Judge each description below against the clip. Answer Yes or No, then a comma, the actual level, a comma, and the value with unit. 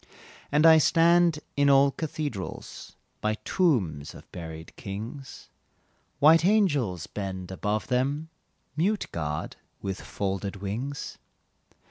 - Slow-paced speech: Yes, slow, 105 wpm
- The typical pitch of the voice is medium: No, low, 130 Hz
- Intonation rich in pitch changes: Yes, wide, 8.2 semitones